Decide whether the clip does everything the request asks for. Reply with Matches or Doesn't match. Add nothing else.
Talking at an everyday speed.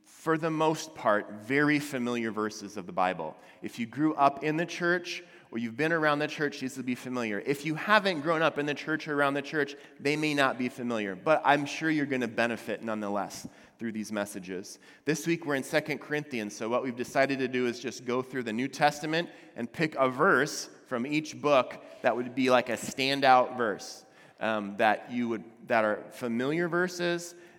Doesn't match